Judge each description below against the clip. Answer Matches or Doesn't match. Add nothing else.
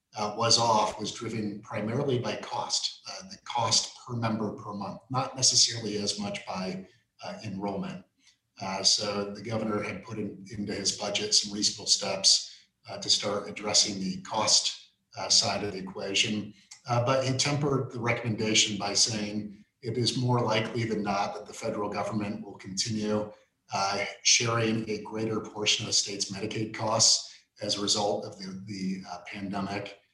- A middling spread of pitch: Doesn't match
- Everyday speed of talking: Matches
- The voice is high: Doesn't match